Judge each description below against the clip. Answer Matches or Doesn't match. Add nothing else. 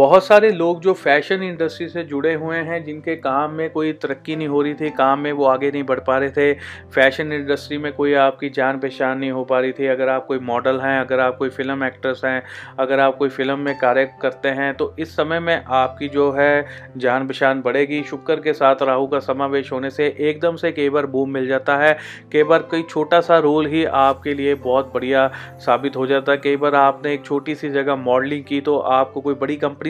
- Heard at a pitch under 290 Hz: Matches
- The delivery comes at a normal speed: Doesn't match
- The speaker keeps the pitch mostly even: Matches